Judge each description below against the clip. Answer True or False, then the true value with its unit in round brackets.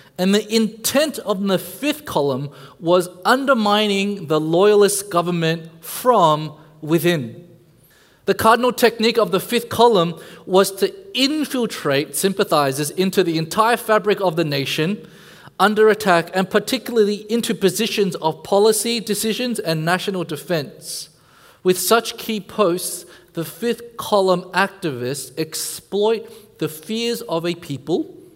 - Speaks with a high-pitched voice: True (195 Hz)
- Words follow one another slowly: True (125 wpm)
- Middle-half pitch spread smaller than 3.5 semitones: False (5.0 semitones)